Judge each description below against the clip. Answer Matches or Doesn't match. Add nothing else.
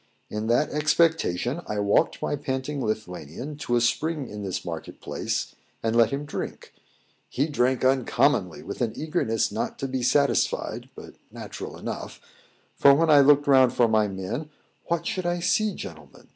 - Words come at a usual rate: Matches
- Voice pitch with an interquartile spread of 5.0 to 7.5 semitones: Matches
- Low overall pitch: Matches